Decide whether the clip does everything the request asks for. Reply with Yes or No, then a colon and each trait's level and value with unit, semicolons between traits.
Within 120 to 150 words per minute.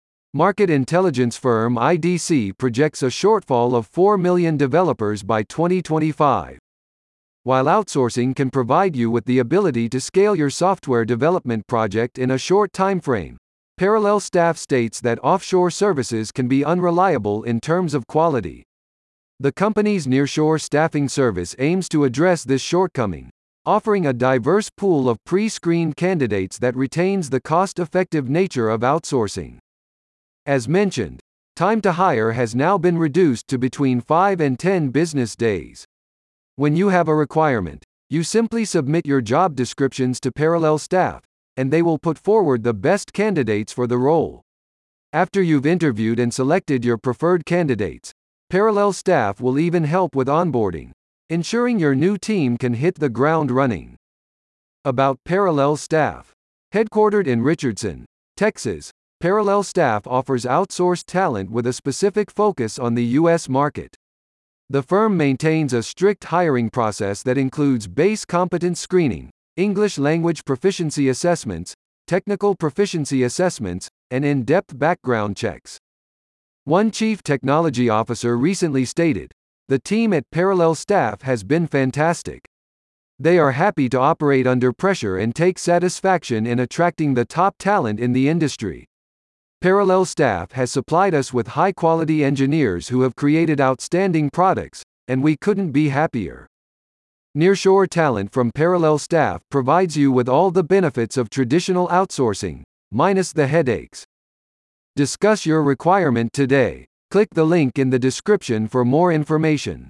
Yes: average, 140 wpm